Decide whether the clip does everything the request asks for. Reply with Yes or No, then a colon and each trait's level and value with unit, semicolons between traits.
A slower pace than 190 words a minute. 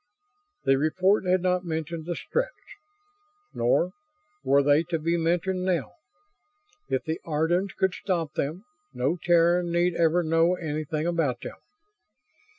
Yes: slow, 135 wpm